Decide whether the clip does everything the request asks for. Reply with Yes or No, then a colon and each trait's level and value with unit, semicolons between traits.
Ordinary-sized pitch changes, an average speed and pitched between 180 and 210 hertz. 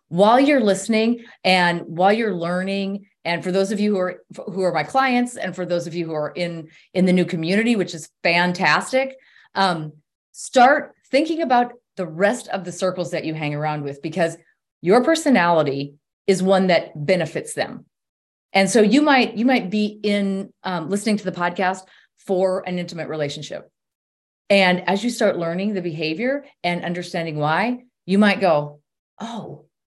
Yes: average, 3.7 semitones; average, 175 wpm; medium, 185 Hz